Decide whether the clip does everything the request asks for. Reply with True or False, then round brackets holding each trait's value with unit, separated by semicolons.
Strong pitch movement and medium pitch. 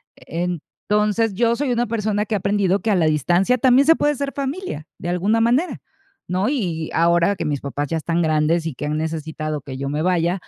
True (6.1 semitones; 180 Hz)